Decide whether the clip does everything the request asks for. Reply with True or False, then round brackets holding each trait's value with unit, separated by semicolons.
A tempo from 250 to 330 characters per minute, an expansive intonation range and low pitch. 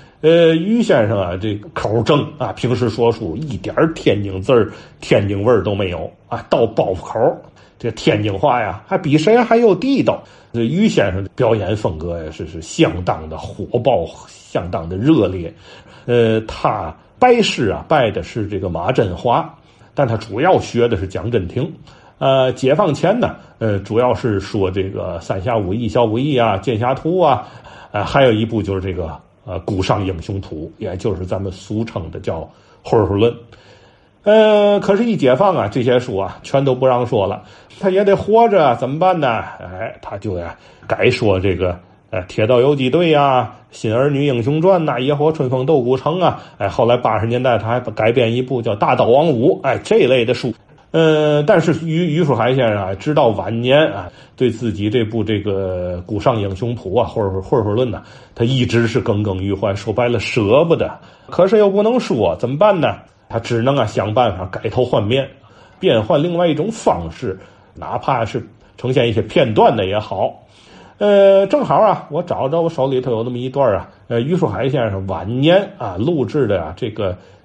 True (265 characters per minute; 6.3 semitones; 120 Hz)